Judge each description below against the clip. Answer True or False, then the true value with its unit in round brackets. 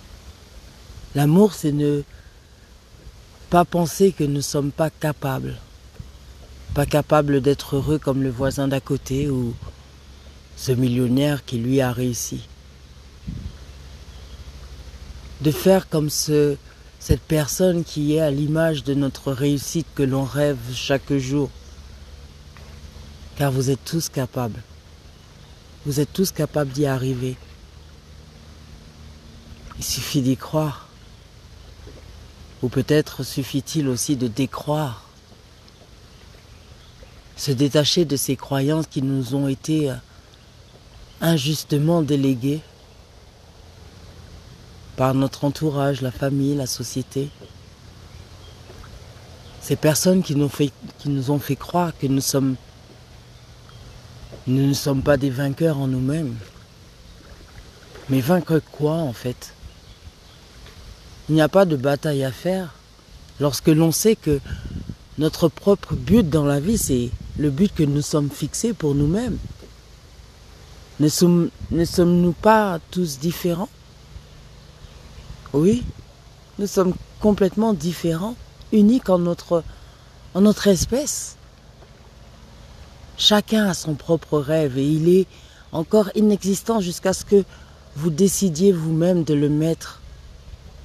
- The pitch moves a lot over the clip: True (8.4 semitones)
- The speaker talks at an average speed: False (115 wpm)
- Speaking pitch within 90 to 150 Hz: True (135 Hz)